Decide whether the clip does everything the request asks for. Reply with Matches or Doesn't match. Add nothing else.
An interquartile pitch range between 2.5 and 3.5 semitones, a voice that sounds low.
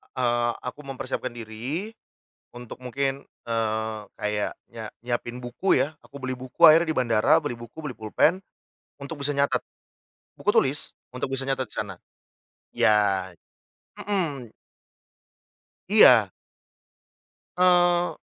Doesn't match